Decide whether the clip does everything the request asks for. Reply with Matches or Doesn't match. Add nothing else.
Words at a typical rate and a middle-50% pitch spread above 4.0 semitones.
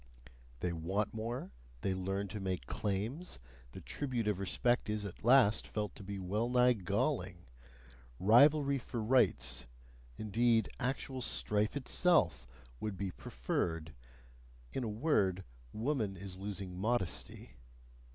Doesn't match